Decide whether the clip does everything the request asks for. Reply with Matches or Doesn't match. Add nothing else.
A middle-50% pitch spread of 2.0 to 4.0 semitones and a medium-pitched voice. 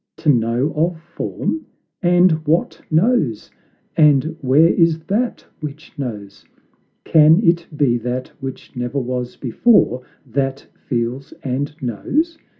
Doesn't match